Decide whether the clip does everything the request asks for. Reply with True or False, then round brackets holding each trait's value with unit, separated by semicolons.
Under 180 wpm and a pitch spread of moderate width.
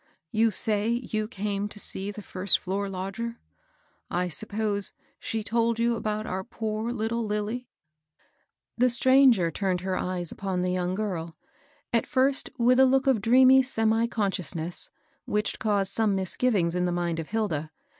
True (160 wpm; 3.8 semitones)